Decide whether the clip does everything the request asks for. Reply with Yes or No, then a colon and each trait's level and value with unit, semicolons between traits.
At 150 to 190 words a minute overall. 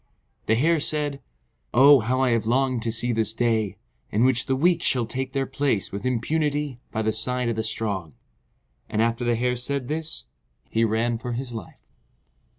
Yes: average, 185 wpm